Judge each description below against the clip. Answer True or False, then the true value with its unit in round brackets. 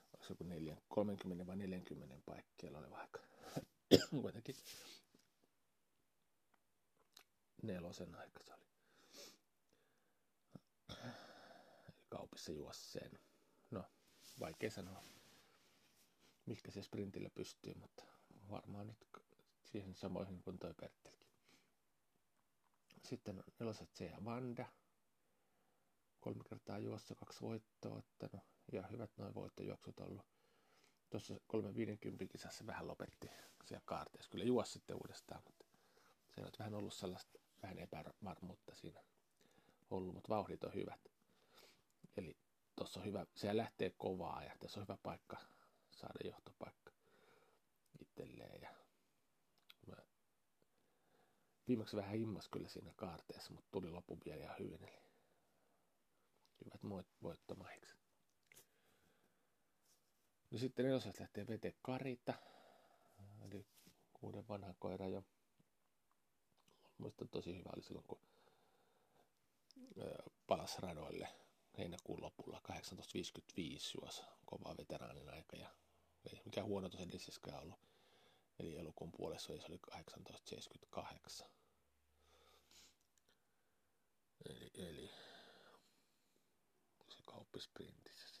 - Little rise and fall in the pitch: False (3.2 semitones)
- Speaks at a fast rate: False (95 wpm)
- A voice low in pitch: True (100 Hz)